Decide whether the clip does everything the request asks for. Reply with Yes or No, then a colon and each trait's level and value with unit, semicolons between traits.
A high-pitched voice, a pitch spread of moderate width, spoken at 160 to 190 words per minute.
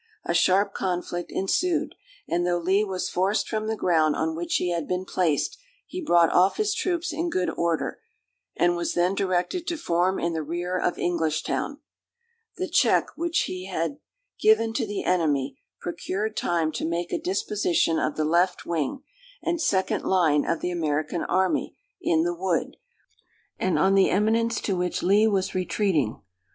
No: medium, 180 Hz; average, 3.4 semitones; average, 170 wpm